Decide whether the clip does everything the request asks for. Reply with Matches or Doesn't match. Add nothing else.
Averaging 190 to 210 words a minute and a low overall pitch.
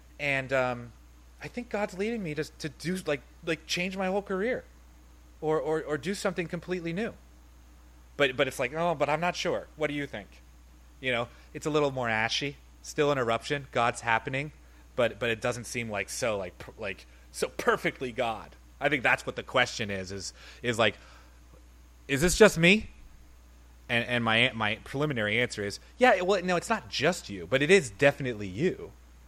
Matches